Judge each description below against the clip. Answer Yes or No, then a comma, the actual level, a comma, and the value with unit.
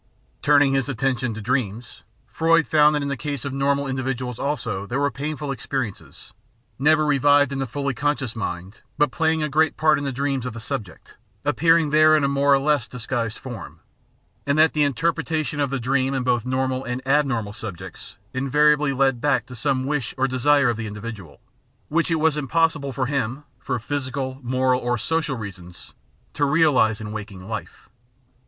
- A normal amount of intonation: Yes, average, 3.3 semitones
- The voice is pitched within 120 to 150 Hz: Yes, low, 135 Hz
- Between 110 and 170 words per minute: No, average, 185 wpm